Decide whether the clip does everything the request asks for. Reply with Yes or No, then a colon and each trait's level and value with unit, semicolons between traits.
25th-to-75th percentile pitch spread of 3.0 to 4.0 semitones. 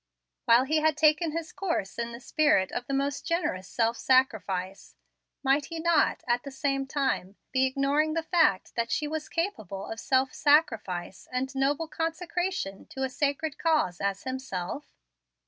No: average, 5.1 semitones